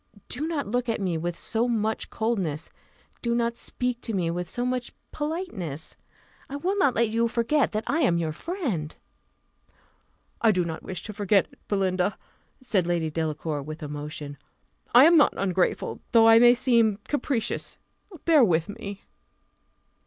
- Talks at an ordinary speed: Yes, average, 160 wpm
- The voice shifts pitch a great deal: Yes, wide, 6.2 semitones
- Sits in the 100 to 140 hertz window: No, high, 220 Hz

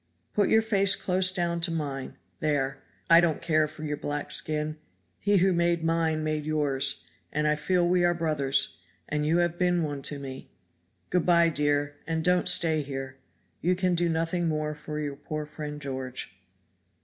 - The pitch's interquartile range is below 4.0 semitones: Yes, average, 2.9 semitones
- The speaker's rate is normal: Yes, average, 180 wpm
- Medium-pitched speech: Yes, medium, 155 Hz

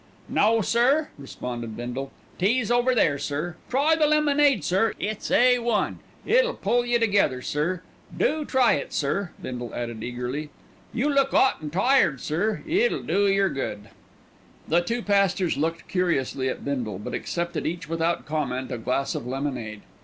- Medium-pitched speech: Yes, medium, 175 Hz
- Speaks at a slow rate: No, average, 160 wpm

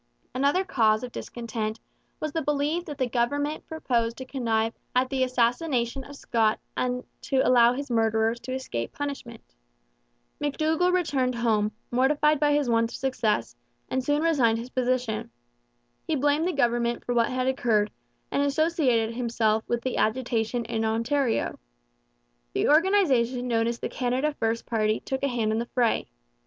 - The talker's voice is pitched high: Yes, very high, 250 Hz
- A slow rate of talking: No, average, 160 wpm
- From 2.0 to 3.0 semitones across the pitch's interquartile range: No, average, 3.6 semitones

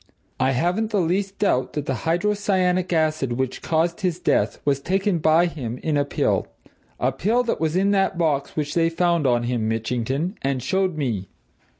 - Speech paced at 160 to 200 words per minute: Yes, average, 185 wpm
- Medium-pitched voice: Yes, medium, 160 Hz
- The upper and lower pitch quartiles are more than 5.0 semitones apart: Yes, wide, 5.5 semitones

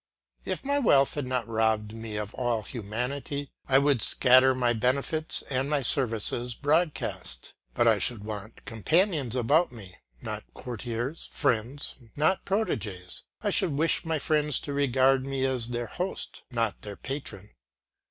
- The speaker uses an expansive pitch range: No, average, 4.2 semitones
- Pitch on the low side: Yes, low, 130 Hz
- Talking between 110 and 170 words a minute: Yes, average, 150 wpm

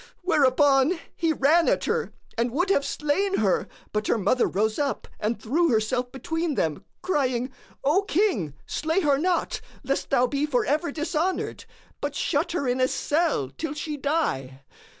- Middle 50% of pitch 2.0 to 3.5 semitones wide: No, average, 4.9 semitones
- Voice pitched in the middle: No, very high, 285 Hz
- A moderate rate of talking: Yes, average, 160 wpm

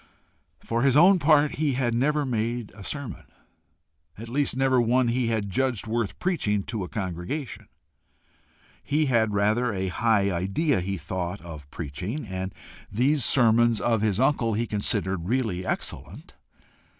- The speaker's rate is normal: Yes, average, 150 wpm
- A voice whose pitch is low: Yes, low, 115 Hz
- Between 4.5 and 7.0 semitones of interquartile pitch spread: Yes, average, 4.9 semitones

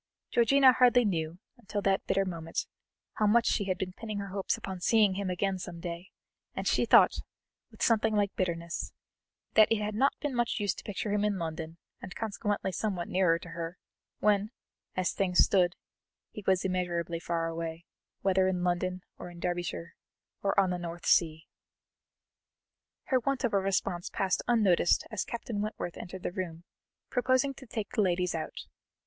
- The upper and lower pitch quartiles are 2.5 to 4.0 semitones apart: Yes, average, 3.3 semitones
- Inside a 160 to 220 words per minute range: Yes, average, 175 wpm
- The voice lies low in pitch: No, high, 190 Hz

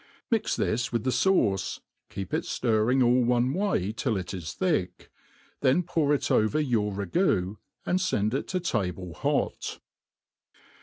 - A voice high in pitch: No, low, 120 Hz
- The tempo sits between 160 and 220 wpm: No, average, 150 wpm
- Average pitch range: No, wide, 6.8 semitones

